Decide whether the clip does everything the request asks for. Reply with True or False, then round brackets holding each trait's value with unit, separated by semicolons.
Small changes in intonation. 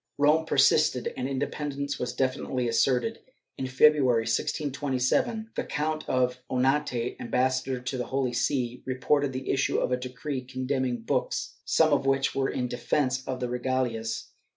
True (2.1 semitones)